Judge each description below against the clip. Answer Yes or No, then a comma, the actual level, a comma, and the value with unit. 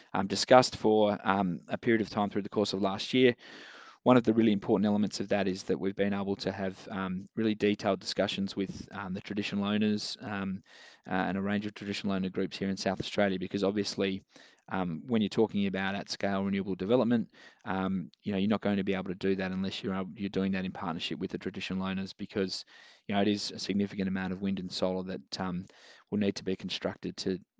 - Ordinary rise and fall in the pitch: No, narrow, 1.5 semitones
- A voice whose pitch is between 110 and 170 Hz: No, low, 100 Hz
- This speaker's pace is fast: Yes, fast, 230 wpm